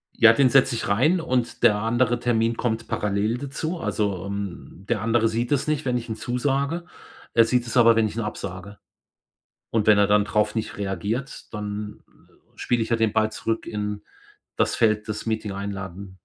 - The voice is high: No, low, 110 Hz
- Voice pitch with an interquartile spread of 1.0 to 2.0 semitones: No, average, 2.8 semitones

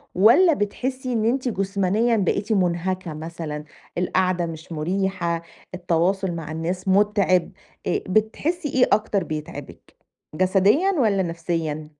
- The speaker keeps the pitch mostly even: No, average, 4.2 semitones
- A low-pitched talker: No, medium, 185 Hz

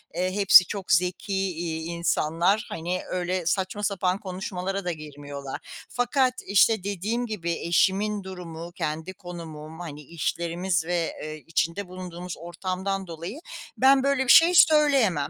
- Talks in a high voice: No, medium, 180 Hz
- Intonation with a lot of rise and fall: No, average, 3.1 semitones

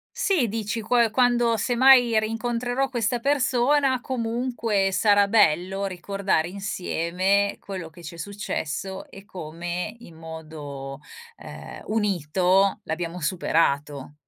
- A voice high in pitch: Yes, high, 200 Hz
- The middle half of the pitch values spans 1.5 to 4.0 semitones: No, wide, 5.6 semitones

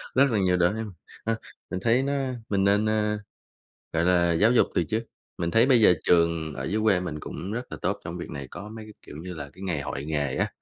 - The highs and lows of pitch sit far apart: No, average, 4.7 semitones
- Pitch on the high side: No, very low, 95 Hz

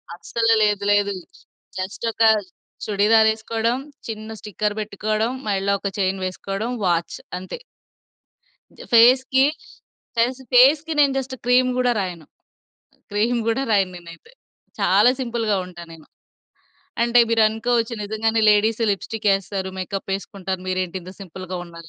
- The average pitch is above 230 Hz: No, high, 215 Hz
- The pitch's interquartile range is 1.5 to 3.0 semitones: No, average, 3.4 semitones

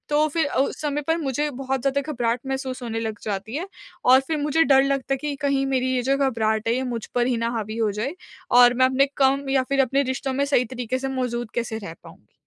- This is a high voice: Yes, very high, 260 Hz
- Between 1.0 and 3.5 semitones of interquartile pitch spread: Yes, narrow, 2.6 semitones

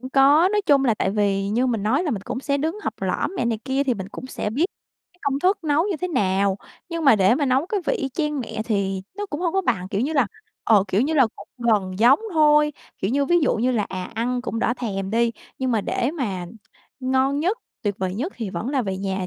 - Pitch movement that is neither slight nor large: No, wide, 6.2 semitones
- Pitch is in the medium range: No, very high, 250 Hz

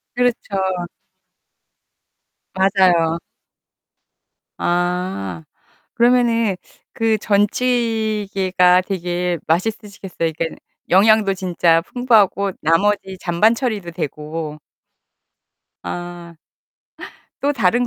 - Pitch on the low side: No, high, 190 Hz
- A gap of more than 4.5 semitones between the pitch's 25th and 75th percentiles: No, average, 4.0 semitones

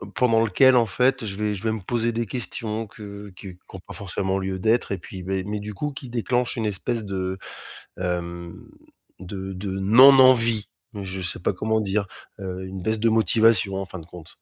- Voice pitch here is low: Yes, low, 105 Hz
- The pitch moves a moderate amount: Yes, average, 3.2 semitones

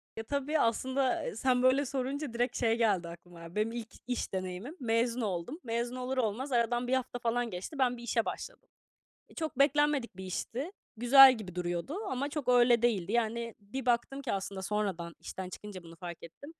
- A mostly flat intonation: No, average, 4.6 semitones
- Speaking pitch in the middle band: No, high, 235 Hz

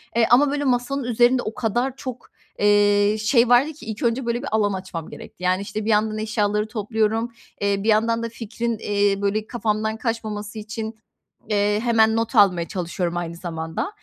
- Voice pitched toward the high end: Yes, high, 220 Hz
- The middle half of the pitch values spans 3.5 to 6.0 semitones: No, narrow, 2.5 semitones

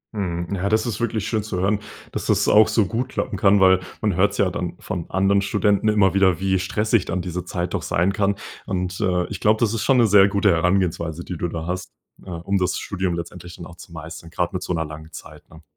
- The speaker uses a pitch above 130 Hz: No, very low, 95 Hz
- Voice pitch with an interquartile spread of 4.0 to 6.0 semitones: No, average, 2.7 semitones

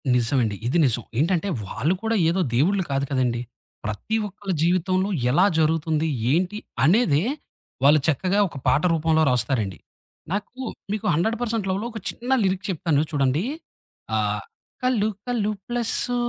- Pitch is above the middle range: No, medium, 165 Hz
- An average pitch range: No, wide, 6.7 semitones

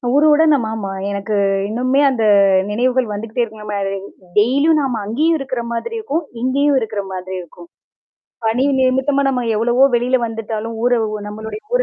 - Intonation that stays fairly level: No, average, 3.9 semitones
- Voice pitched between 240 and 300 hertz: Yes, high, 245 Hz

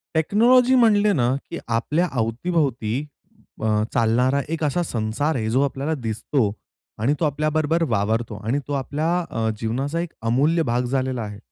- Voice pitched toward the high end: No, low, 135 Hz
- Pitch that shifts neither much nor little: No, wide, 5.8 semitones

